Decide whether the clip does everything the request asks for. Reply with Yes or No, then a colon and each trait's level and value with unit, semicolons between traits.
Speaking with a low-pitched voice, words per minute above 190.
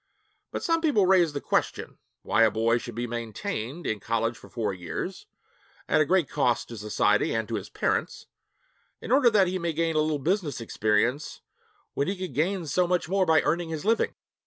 No: medium, 155 Hz; average, 200 wpm